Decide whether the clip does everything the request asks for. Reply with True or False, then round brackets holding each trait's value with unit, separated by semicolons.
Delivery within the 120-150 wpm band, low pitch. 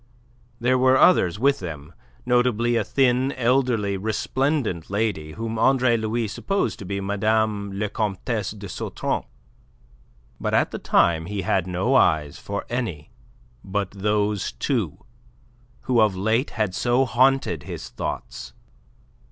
True (135 wpm; 110 Hz)